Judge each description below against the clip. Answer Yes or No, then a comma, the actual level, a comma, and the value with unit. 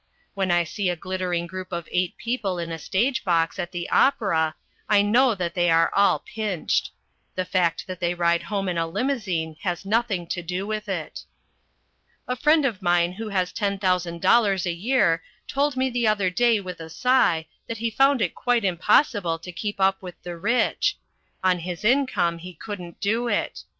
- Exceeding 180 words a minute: Yes, average, 190 wpm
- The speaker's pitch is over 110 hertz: Yes, medium, 185 Hz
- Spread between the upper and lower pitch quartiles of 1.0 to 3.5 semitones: No, average, 4.3 semitones